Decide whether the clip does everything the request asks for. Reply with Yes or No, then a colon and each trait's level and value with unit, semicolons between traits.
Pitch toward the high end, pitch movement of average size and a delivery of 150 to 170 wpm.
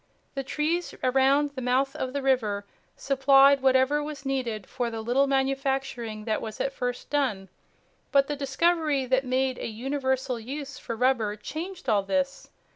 No: very high, 265 Hz; narrow, 2.1 semitones; average, 160 wpm